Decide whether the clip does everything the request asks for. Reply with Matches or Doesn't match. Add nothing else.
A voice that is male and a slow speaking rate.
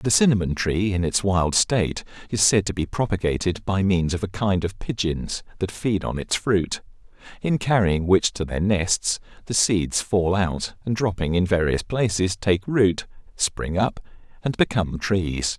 Doesn't match